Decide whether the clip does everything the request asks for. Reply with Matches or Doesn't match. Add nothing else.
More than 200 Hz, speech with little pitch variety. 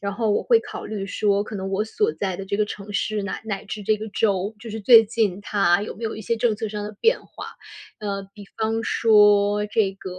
Matches